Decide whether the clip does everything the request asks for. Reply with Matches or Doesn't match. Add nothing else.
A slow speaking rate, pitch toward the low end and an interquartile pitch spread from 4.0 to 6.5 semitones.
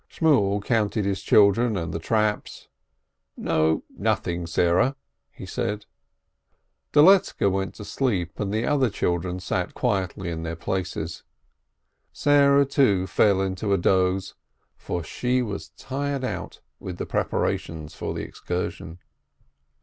Matches